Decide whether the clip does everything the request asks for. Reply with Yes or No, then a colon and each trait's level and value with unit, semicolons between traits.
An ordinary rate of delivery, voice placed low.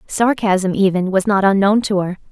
No: average, 180 wpm; high, 200 Hz